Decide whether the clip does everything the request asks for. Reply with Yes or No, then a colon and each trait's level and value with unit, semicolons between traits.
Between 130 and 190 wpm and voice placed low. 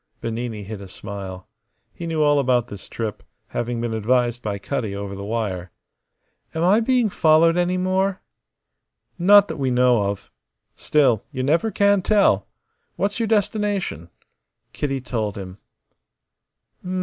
Yes: average, 140 wpm; low, 125 Hz